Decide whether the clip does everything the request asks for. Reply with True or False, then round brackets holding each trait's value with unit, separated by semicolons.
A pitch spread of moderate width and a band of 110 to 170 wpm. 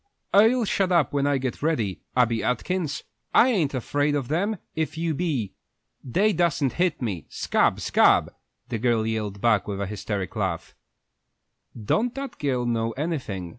False (7.3 semitones; 160 wpm)